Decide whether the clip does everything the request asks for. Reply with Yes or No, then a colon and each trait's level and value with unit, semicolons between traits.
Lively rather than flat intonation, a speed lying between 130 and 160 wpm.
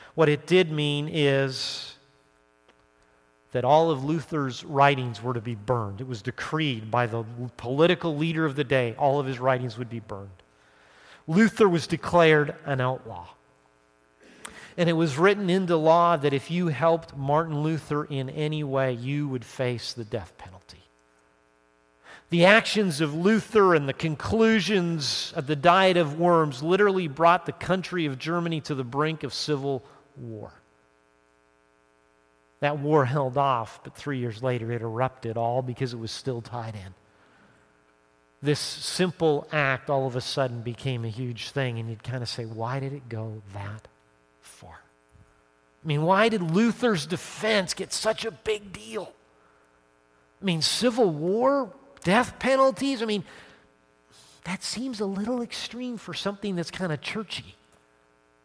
Yes: wide, 7.7 semitones; average, 155 wpm